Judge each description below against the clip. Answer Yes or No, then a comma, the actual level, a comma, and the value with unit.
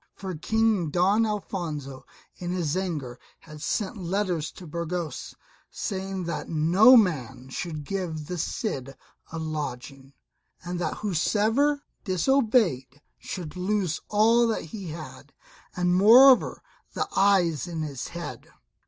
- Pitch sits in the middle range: Yes, medium, 180 Hz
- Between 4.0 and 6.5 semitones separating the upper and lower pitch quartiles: Yes, average, 4.9 semitones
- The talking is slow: Yes, slow, 125 wpm